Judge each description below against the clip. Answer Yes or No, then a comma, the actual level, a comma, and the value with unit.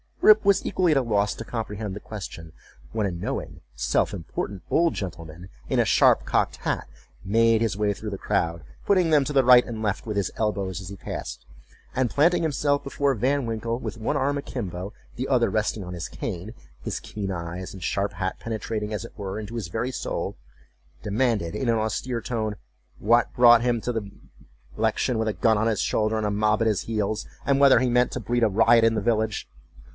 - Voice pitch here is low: Yes, low, 110 Hz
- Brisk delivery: Yes, fast, 210 wpm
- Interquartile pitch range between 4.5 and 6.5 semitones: No, average, 3.3 semitones